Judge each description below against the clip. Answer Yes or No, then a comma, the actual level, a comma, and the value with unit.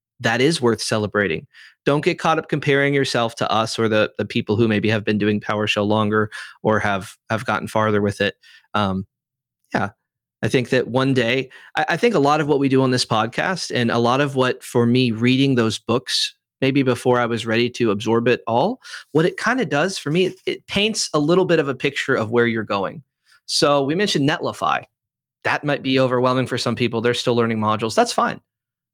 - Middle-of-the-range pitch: No, low, 120 Hz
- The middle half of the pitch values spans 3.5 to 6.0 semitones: Yes, average, 4.4 semitones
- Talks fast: Yes, fast, 220 wpm